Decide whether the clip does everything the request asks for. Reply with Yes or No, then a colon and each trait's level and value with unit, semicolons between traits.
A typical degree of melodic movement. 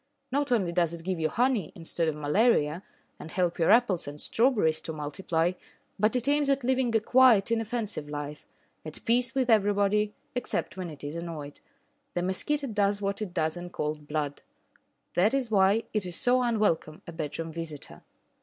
No: wide, 6.3 semitones